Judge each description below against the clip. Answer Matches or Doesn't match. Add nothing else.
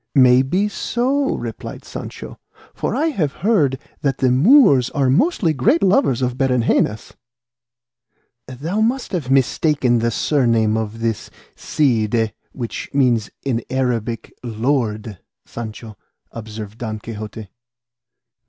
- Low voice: Matches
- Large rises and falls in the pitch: Doesn't match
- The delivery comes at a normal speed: Doesn't match